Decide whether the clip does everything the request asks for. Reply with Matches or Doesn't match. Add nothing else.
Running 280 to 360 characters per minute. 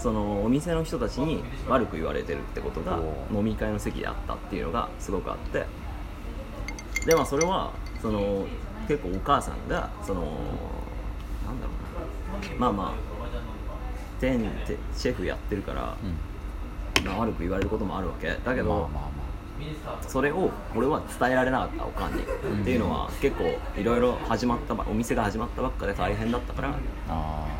Matches